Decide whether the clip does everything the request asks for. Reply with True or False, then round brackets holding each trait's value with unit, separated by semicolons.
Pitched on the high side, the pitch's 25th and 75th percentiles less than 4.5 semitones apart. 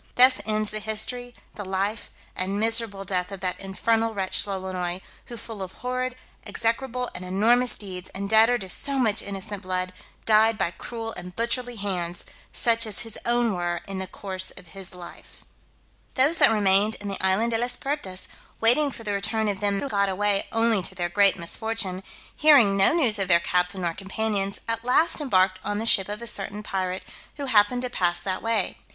True (205 Hz; 3.3 semitones)